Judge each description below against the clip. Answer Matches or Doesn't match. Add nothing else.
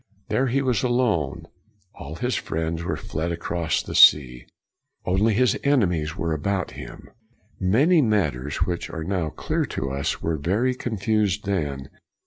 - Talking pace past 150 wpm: Doesn't match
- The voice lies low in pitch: Matches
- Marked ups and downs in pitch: Matches